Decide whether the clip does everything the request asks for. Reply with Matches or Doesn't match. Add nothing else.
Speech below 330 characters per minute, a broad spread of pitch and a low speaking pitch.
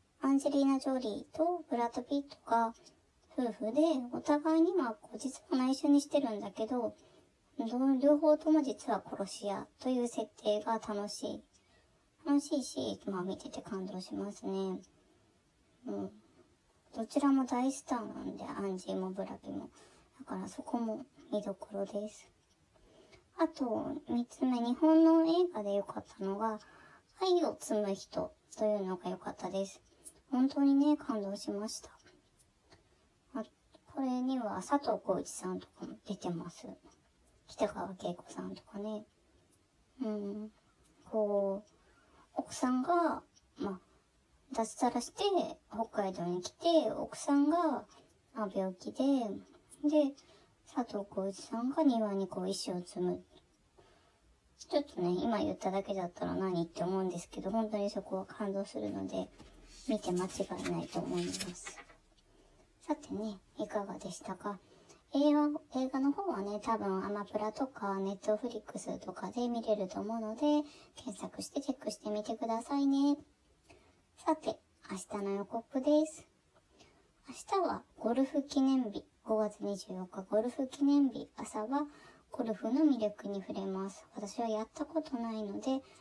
Doesn't match